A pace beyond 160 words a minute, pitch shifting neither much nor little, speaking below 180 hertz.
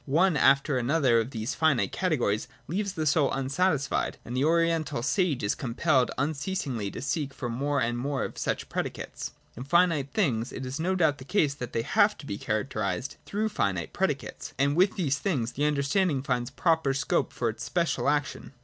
Yes: average, 190 wpm; average, 4.7 semitones; medium, 140 Hz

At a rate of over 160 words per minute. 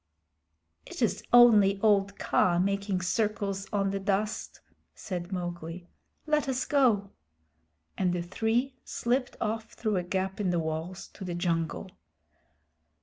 No: slow, 135 wpm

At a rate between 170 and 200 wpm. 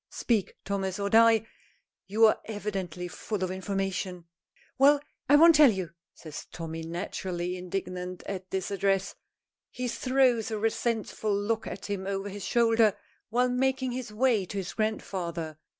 No: average, 150 wpm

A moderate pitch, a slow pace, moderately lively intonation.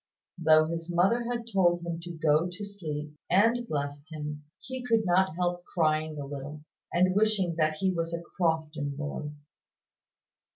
No: medium, 170 Hz; average, 160 wpm; average, 3.6 semitones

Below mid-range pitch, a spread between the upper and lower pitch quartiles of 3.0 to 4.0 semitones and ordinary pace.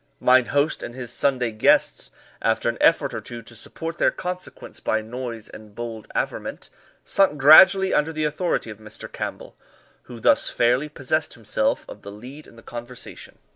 No: low, 125 Hz; average, 4.7 semitones; average, 175 wpm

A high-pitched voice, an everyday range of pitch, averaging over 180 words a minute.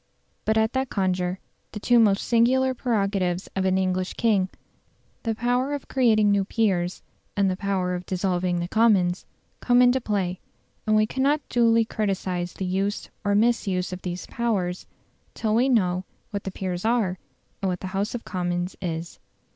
No: high, 200 Hz; average, 3.9 semitones; average, 170 wpm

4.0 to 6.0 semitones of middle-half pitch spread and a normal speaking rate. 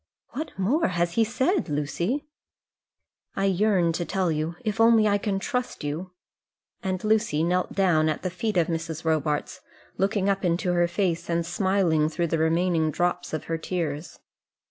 No: average, 3.4 semitones; average, 165 wpm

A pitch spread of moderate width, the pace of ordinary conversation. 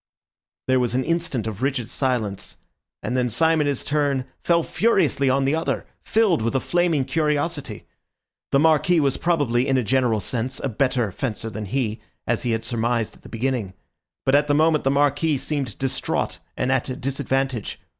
Yes: average, 3.6 semitones; average, 185 wpm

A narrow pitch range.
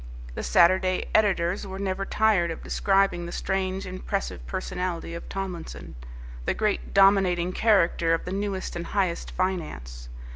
Yes: narrow, 2.2 semitones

